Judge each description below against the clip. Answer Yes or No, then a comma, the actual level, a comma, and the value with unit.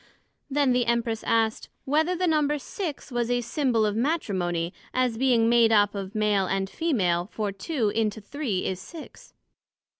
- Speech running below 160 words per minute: No, average, 170 wpm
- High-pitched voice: Yes, high, 230 Hz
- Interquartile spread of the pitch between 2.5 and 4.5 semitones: No, average, 5.1 semitones